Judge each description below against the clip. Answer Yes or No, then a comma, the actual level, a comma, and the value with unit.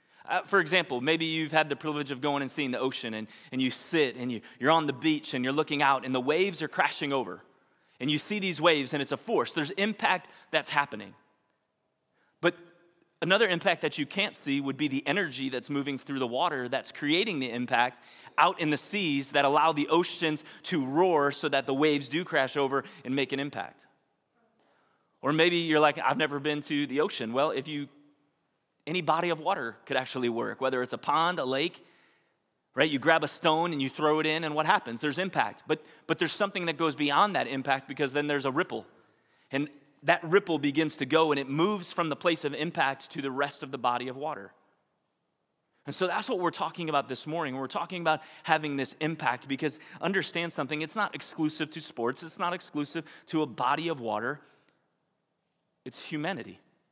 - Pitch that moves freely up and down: No, average, 3.0 semitones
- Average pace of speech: No, fast, 210 wpm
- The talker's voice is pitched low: No, medium, 150 Hz